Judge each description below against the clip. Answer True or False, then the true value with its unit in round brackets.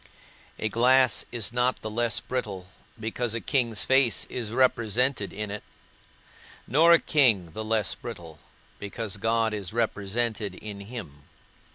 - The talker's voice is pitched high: False (110 Hz)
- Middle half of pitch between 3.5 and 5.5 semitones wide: False (3.1 semitones)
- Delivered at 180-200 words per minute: False (140 wpm)